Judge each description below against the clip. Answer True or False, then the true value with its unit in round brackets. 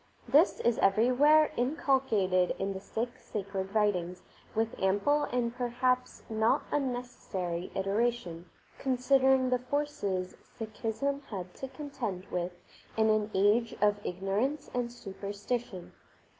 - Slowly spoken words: True (115 wpm)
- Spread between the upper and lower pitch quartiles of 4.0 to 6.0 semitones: True (4.6 semitones)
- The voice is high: True (225 Hz)